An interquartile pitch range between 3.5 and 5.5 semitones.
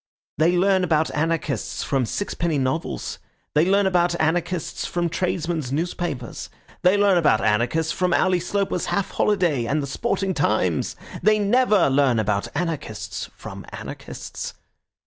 Yes: average, 4.7 semitones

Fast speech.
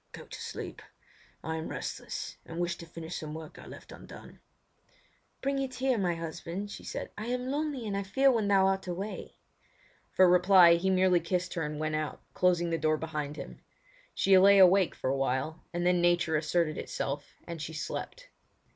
No: average, 190 wpm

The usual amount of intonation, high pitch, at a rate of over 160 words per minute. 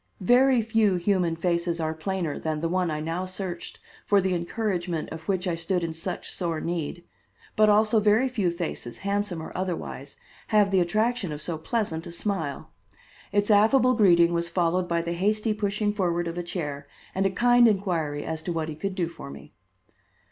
No: average, 3.7 semitones; medium, 180 Hz; average, 190 wpm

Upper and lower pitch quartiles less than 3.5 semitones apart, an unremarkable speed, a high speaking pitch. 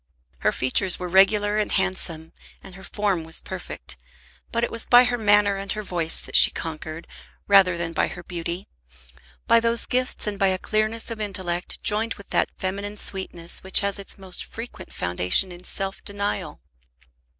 Yes: average, 3.1 semitones; average, 175 wpm; high, 195 Hz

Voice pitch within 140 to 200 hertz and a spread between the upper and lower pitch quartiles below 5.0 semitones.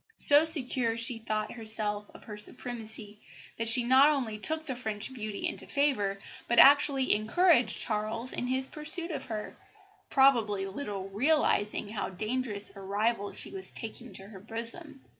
No: high, 230 Hz; average, 4.2 semitones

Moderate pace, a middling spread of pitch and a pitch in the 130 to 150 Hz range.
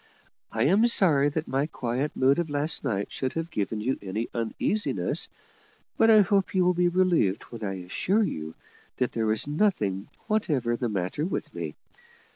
No: average, 175 wpm; wide, 8.6 semitones; medium, 140 Hz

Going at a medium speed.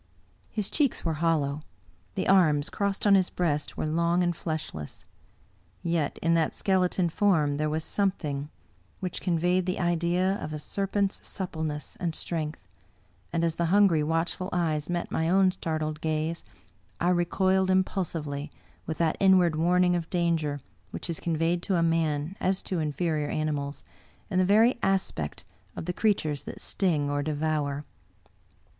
Yes: average, 155 wpm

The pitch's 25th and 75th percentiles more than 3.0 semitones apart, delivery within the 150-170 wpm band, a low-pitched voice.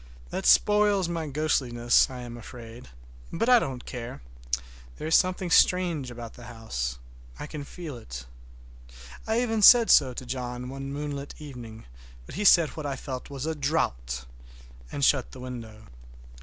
Yes: wide, 5.6 semitones; average, 155 wpm; low, 130 Hz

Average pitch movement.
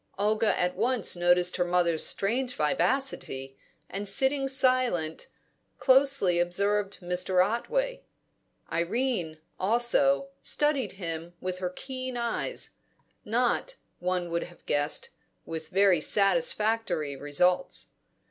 No: wide, 6.5 semitones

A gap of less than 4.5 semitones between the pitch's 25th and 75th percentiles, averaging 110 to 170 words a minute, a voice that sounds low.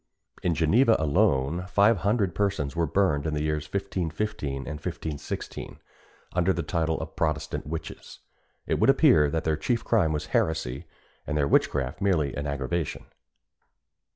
Yes: average, 4.0 semitones; average, 150 wpm; very low, 80 Hz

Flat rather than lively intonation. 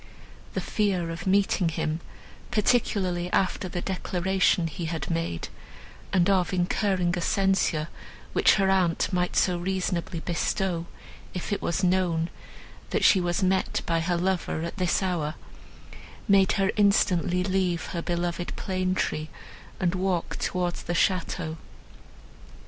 Yes: narrow, 1.9 semitones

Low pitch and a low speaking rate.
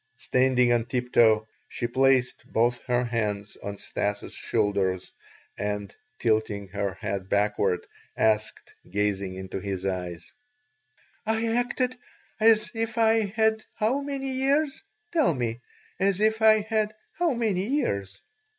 Yes: low, 125 Hz; slow, 125 wpm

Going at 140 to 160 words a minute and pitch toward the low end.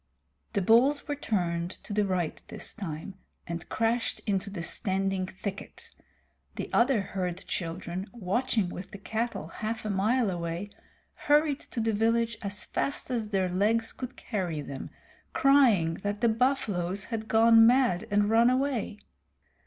No: average, 150 wpm; high, 210 Hz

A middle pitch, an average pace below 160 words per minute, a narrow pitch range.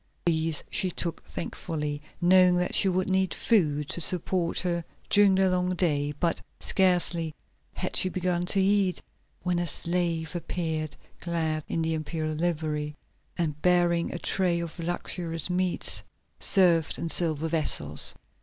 Yes: medium, 170 Hz; average, 145 wpm; narrow, 2.2 semitones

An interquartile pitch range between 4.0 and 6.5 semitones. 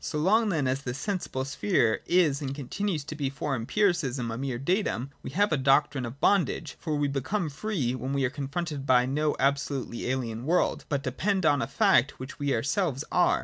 Yes: average, 4.5 semitones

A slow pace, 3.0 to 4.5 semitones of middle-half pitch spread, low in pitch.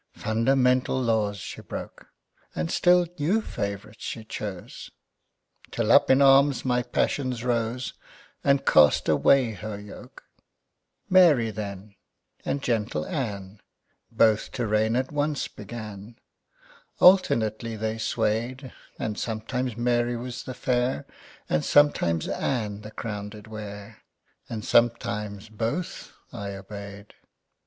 Yes: slow, 115 wpm; average, 3.5 semitones; low, 110 Hz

